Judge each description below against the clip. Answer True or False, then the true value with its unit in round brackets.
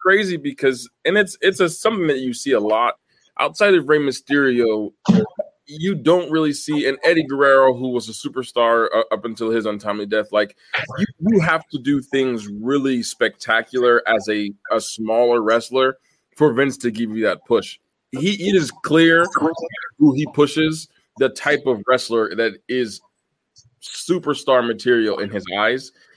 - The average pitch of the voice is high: False (135 Hz)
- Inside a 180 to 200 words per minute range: False (165 wpm)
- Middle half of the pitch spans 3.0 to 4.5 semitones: False (5.3 semitones)